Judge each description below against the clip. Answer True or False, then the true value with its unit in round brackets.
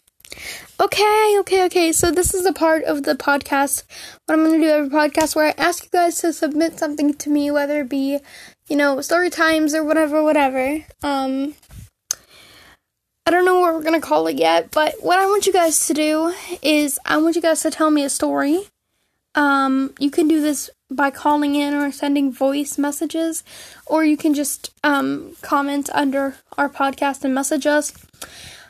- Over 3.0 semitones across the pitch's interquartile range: False (2.4 semitones)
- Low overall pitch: False (300 Hz)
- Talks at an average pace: True (190 wpm)